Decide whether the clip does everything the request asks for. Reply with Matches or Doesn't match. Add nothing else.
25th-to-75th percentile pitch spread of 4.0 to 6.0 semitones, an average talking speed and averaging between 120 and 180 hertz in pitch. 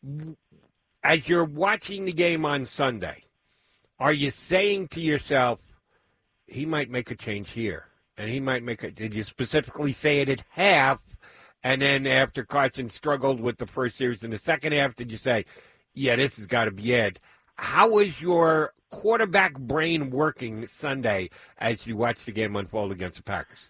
Matches